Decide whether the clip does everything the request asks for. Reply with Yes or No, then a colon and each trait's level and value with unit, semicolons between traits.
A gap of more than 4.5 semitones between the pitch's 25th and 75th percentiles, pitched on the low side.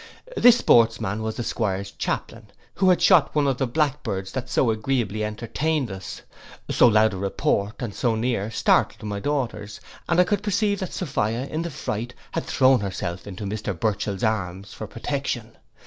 Yes: average, 5.2 semitones; low, 115 Hz